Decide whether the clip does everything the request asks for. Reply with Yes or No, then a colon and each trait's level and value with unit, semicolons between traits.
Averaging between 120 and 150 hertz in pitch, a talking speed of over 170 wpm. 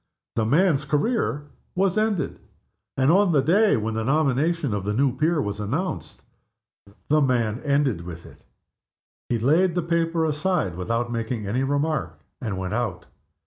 No: medium, 140 Hz; average, 155 wpm